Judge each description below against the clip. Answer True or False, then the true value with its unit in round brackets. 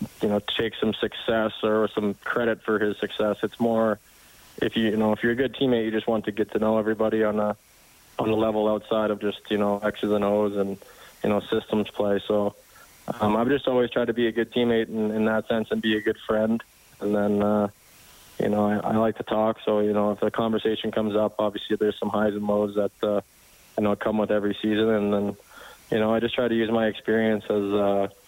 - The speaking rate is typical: False (240 wpm)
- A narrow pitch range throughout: True (1.1 semitones)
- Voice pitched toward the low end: True (105 Hz)